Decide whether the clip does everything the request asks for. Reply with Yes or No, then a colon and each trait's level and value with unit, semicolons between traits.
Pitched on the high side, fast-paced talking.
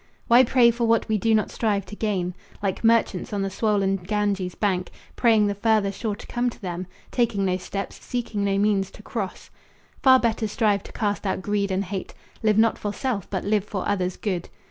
Yes: high, 205 Hz; fast, 210 wpm